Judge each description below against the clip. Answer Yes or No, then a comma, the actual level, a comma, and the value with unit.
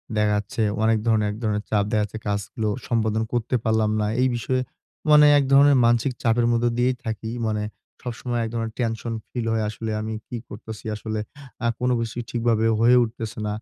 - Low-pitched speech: Yes, low, 115 Hz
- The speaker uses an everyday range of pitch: No, narrow, 1.7 semitones